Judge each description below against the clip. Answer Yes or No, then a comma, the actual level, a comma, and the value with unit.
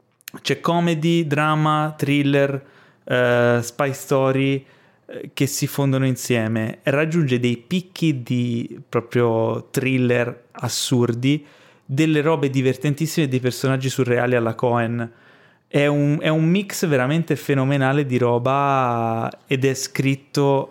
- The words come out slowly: Yes, slow, 110 wpm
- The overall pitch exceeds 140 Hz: No, low, 135 Hz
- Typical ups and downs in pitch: Yes, average, 3.3 semitones